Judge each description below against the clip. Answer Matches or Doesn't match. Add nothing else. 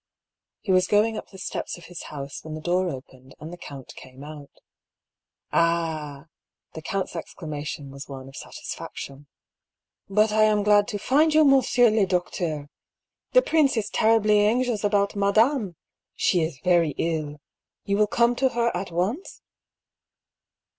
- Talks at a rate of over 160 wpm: Matches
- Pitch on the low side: Doesn't match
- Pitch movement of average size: Doesn't match